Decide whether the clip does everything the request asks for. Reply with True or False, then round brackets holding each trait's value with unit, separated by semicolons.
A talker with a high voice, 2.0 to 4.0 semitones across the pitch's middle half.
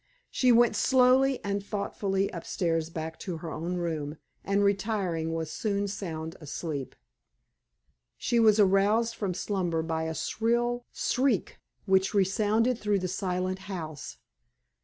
False (195 Hz; 4.6 semitones)